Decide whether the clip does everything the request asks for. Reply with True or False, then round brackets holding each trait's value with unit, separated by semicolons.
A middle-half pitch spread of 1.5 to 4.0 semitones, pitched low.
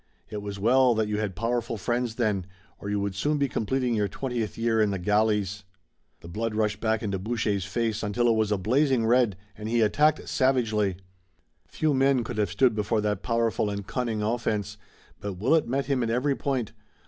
True (2.9 semitones; 110 Hz)